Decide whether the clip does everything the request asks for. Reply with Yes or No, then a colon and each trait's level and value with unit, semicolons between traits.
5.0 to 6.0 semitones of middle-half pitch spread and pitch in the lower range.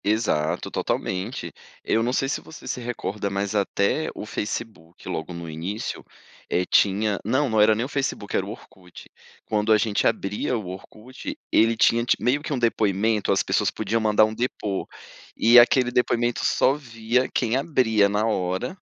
No: average, 3.4 semitones; low, 110 Hz